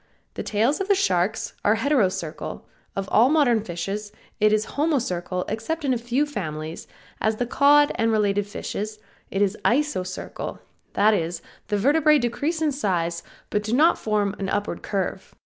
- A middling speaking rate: Yes, average, 160 wpm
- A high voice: Yes, high, 215 Hz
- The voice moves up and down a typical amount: No, wide, 6.3 semitones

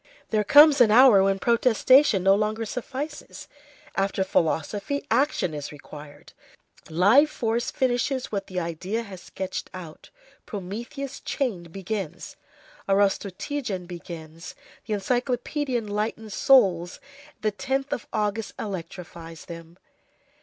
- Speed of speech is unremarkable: No, slow, 110 wpm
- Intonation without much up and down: No, wide, 5.4 semitones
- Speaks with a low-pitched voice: No, high, 205 Hz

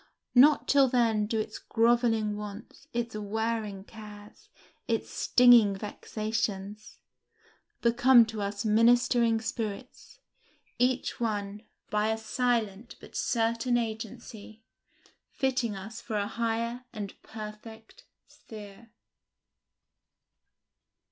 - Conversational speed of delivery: No, slow, 95 wpm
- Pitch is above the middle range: Yes, high, 225 Hz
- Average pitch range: No, narrow, 2.1 semitones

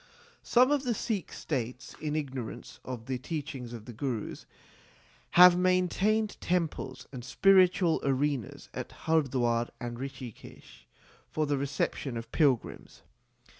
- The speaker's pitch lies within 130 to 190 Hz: Yes, medium, 140 Hz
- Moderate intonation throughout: No, wide, 6.1 semitones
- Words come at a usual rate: No, slow, 125 wpm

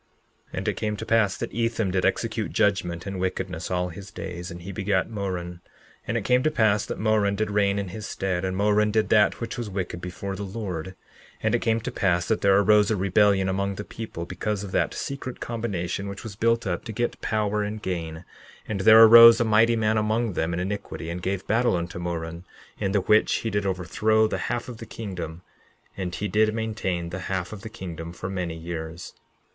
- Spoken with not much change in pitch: No, average, 3.4 semitones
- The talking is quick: Yes, fast, 215 wpm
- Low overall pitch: Yes, low, 100 Hz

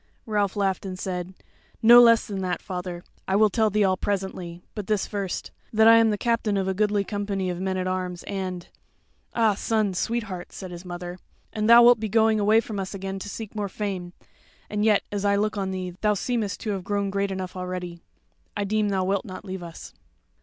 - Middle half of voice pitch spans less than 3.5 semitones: Yes, narrow, 2.4 semitones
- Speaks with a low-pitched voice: No, high, 200 Hz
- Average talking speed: No, fast, 215 wpm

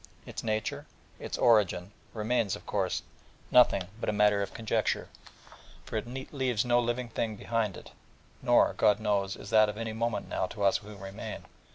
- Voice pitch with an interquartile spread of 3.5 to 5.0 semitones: No, narrow, 2.4 semitones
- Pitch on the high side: No, low, 110 Hz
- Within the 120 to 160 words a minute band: No, average, 170 wpm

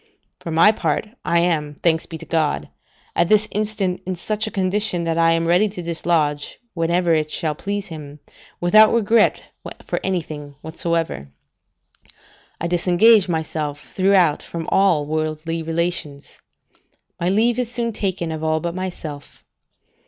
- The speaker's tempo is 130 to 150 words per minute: Yes, average, 145 wpm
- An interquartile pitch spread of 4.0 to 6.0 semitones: No, average, 3.5 semitones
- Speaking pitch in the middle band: Yes, medium, 170 Hz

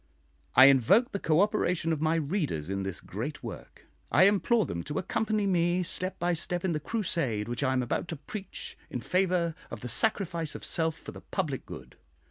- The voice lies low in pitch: No, medium, 165 Hz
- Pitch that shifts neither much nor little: No, wide, 6.0 semitones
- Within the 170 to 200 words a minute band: Yes, average, 195 wpm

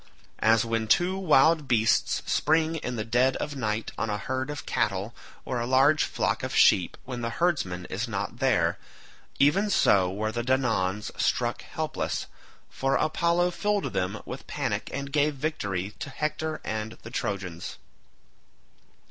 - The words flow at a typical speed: Yes, average, 150 wpm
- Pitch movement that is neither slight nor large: No, wide, 6.0 semitones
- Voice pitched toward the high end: No, low, 125 Hz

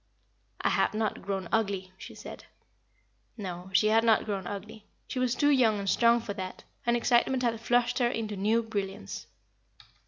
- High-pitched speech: Yes, high, 220 Hz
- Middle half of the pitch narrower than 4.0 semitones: Yes, average, 3.2 semitones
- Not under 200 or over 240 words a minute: No, average, 175 wpm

